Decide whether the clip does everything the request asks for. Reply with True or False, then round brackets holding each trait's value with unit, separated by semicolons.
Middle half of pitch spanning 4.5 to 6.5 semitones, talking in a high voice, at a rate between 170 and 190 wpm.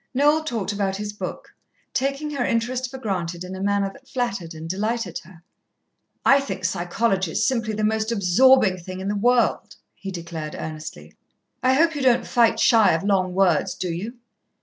True (5.0 semitones; 205 Hz; 180 wpm)